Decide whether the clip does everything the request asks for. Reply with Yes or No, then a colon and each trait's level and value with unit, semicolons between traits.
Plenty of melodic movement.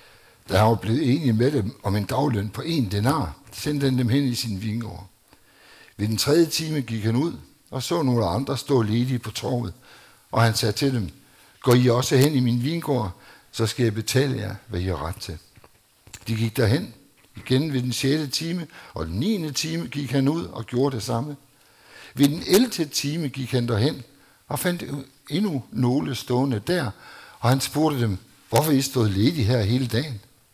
No: average, 3.9 semitones